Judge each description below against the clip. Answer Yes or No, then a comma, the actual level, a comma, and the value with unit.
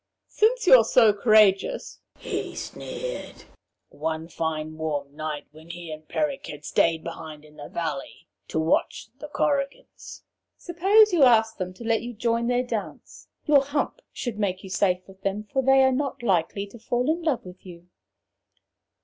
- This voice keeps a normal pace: Yes, average, 165 wpm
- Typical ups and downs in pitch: No, wide, 8.5 semitones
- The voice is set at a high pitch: Yes, high, 215 Hz